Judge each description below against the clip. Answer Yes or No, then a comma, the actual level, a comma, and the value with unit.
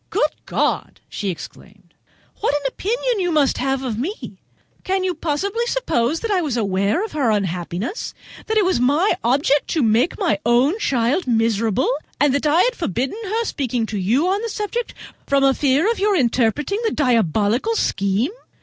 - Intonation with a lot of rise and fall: Yes, wide, 8.7 semitones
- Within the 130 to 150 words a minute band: No, average, 175 wpm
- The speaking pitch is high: Yes, very high, 280 Hz